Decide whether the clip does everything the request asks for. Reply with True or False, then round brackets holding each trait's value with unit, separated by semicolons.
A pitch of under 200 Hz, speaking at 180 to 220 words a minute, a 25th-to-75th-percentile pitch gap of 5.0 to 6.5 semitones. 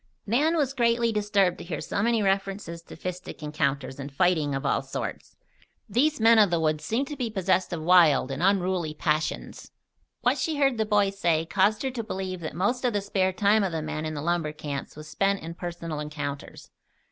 True (185 Hz; 205 wpm; 5.3 semitones)